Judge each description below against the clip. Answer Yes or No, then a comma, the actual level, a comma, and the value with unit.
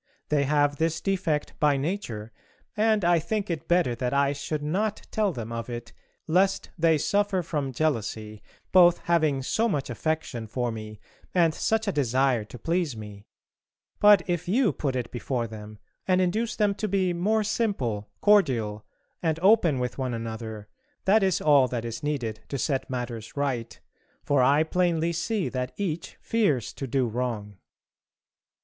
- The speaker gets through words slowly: No, average, 165 wpm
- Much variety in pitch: Yes, wide, 7.0 semitones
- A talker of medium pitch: Yes, medium, 145 Hz